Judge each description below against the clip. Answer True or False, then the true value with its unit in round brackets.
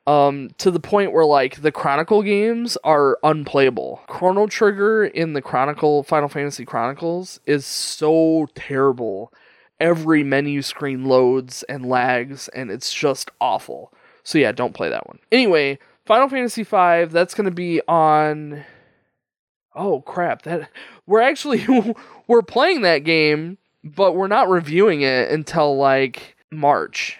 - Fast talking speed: False (140 wpm)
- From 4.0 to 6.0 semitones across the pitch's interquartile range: True (4.9 semitones)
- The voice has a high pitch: False (155 Hz)